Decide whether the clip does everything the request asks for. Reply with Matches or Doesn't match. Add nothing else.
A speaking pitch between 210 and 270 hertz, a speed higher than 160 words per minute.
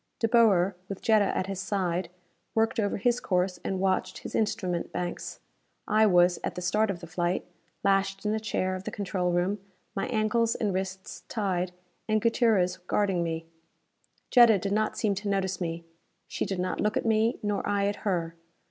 Doesn't match